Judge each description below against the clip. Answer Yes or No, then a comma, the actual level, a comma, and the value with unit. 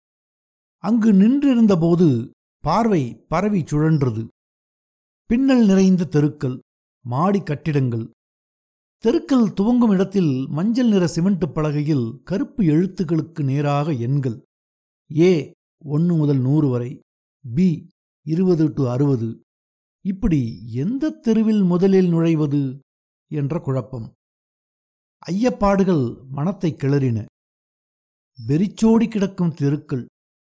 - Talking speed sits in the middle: Yes, average, 85 wpm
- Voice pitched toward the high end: No, medium, 155 Hz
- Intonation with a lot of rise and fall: Yes, wide, 6.5 semitones